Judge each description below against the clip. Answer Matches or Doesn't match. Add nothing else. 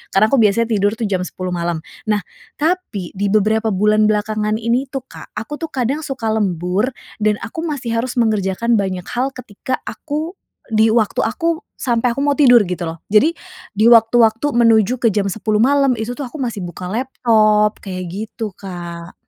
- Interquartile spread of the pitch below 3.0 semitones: Doesn't match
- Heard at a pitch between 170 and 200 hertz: Doesn't match